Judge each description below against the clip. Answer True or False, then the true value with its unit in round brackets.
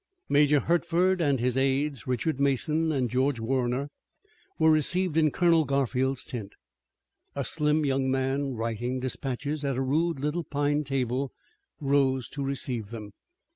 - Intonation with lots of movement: False (2.7 semitones)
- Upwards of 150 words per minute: False (140 wpm)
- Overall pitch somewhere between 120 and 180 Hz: True (135 Hz)